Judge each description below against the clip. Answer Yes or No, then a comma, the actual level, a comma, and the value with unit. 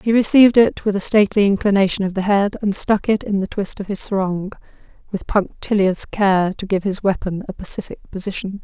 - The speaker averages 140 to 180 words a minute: No, average, 200 wpm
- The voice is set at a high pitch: Yes, high, 200 Hz